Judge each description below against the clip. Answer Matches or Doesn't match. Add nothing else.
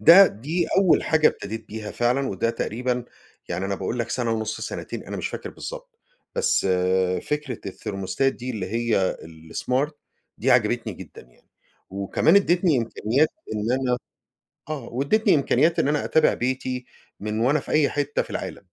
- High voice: Doesn't match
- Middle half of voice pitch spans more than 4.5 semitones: Matches